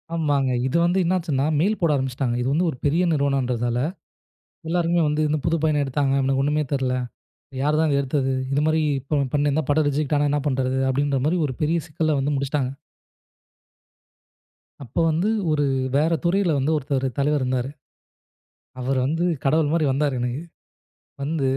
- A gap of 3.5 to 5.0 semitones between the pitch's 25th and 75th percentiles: No, average, 2.7 semitones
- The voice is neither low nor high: Yes, medium, 145 Hz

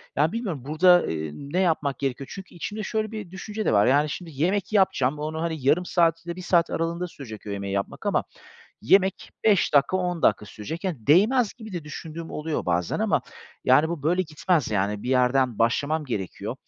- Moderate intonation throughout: No, wide, 5.8 semitones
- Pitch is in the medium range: Yes, medium, 160 Hz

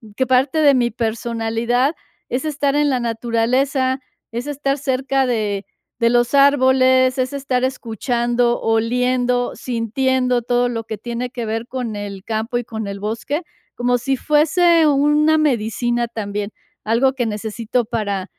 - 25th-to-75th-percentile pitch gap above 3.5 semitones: No, average, 2.7 semitones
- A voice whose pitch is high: Yes, high, 245 Hz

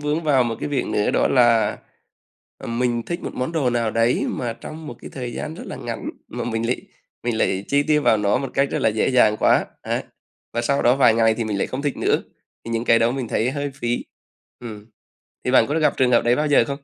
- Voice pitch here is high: No, low, 120 Hz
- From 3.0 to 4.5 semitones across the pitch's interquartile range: Yes, average, 3.4 semitones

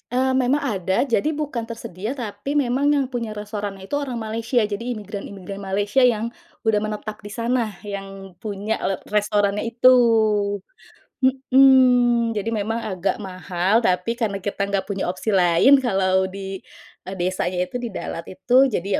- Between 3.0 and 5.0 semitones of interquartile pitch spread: Yes, average, 3.9 semitones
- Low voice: No, high, 210 Hz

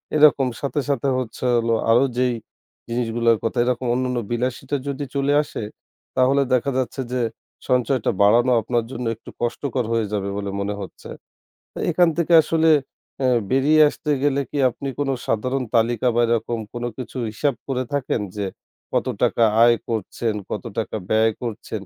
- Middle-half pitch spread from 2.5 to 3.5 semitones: Yes, average, 3.0 semitones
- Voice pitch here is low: Yes, low, 125 Hz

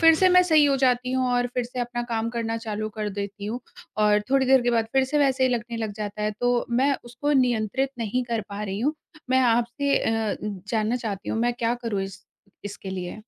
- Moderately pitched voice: No, high, 235 Hz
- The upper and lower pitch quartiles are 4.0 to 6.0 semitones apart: No, average, 3.3 semitones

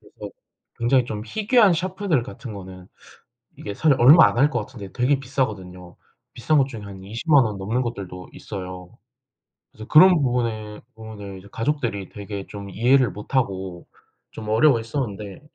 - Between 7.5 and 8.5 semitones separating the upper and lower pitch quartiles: No, average, 5.2 semitones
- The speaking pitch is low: Yes, low, 115 Hz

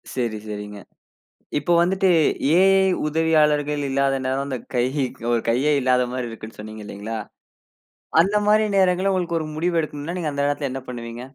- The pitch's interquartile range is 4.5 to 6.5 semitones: Yes, average, 5.2 semitones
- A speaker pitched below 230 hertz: Yes, medium, 140 Hz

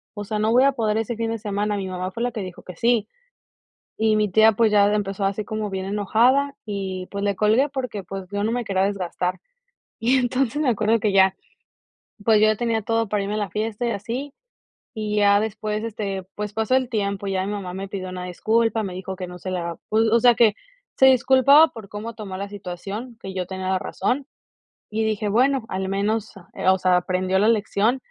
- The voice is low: No, high, 210 Hz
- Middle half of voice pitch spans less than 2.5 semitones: No, average, 2.8 semitones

